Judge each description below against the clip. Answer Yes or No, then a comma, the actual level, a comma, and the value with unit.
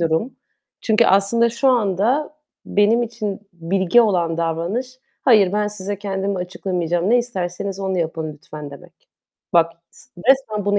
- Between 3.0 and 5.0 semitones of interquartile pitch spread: Yes, average, 4.4 semitones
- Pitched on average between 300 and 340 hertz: No, high, 195 Hz